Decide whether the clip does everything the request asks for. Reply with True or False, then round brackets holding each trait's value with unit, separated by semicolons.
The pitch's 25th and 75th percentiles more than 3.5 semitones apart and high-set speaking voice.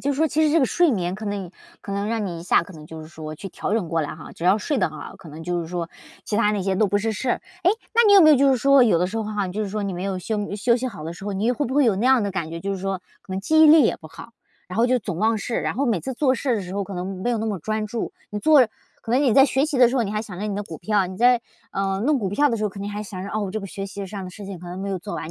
True (4.4 semitones; 205 Hz)